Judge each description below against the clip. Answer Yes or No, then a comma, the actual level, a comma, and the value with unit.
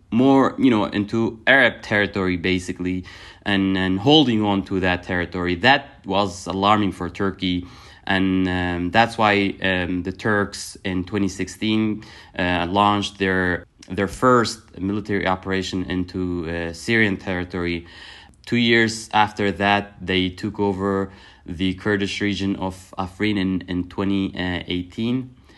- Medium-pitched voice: No, very low, 95 Hz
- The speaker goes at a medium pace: No, slow, 125 wpm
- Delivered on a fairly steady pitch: Yes, narrow, 2.2 semitones